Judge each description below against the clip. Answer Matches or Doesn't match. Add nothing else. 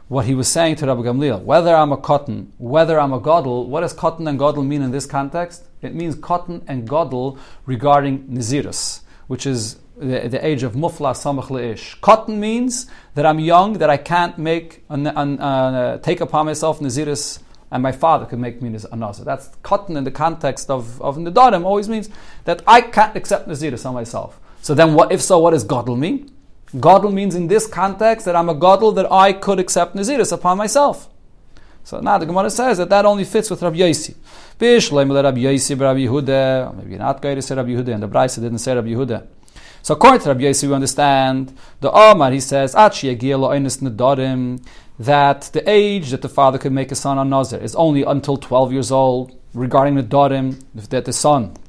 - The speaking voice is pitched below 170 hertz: Matches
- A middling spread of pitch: Matches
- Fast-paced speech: Doesn't match